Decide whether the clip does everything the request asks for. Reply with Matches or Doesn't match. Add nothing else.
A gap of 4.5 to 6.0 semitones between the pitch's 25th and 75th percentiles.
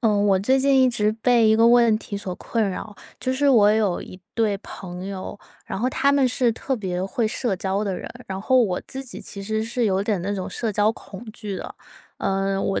Doesn't match